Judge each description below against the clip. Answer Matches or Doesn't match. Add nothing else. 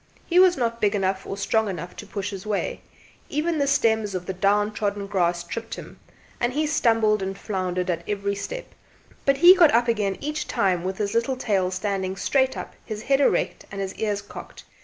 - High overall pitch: Matches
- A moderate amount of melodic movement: Matches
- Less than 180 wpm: Doesn't match